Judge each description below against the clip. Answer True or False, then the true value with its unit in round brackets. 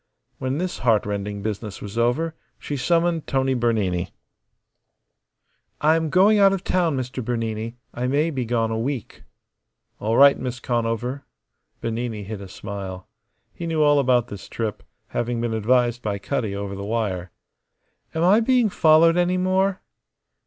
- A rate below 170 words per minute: True (150 wpm)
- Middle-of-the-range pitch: False (120 Hz)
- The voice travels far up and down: True (6.3 semitones)